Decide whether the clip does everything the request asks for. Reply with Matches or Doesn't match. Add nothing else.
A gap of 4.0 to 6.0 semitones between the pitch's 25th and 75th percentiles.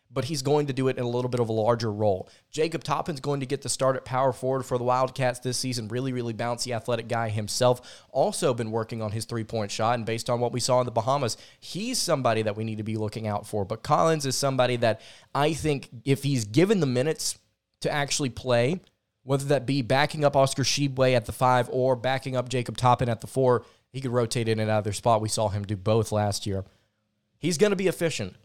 Doesn't match